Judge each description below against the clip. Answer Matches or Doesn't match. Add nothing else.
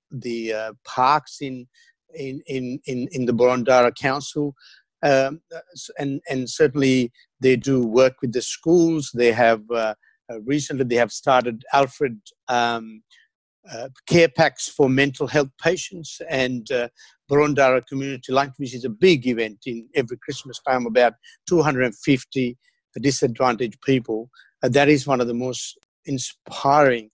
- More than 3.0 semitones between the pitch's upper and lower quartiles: Doesn't match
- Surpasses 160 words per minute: Doesn't match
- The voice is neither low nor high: Doesn't match